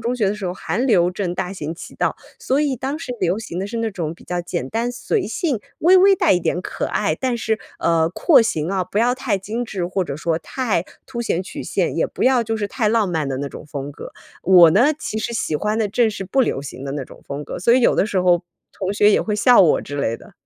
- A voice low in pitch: No, high, 200 Hz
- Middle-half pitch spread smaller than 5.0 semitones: No, wide, 5.4 semitones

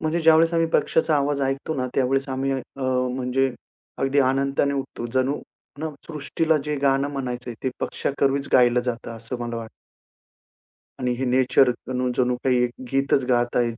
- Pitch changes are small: Yes, narrow, 2.0 semitones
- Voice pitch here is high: No, low, 135 Hz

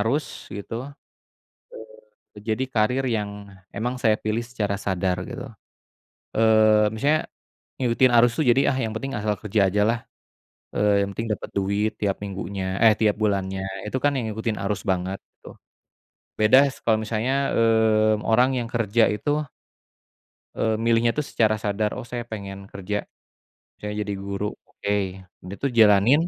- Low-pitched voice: Yes, low, 110 Hz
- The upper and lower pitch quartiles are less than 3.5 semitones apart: Yes, narrow, 2.5 semitones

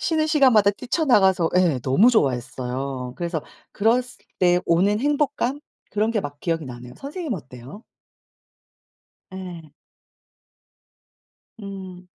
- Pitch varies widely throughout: Yes, wide, 8.7 semitones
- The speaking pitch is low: No, medium, 185 Hz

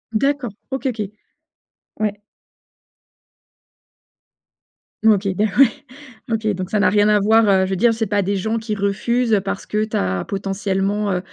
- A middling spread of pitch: No, narrow, 2.2 semitones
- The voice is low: No, high, 210 Hz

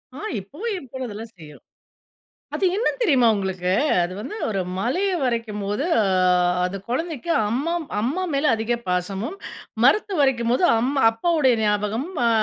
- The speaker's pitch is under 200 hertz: No, high, 240 Hz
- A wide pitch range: Yes, wide, 6.5 semitones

